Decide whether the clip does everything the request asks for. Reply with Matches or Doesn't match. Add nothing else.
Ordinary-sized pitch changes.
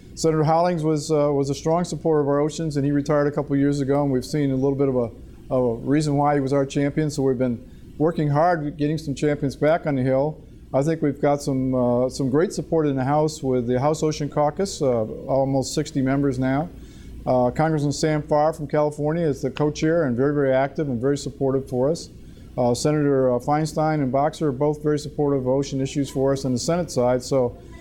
Doesn't match